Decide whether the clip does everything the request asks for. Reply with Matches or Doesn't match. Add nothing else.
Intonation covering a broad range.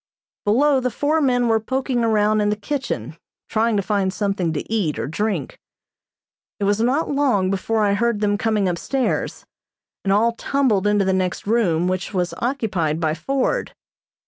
Doesn't match